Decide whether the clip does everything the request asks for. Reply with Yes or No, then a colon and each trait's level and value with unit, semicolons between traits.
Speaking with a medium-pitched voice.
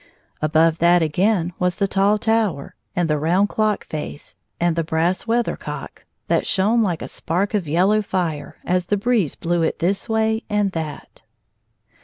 Yes: medium, 180 Hz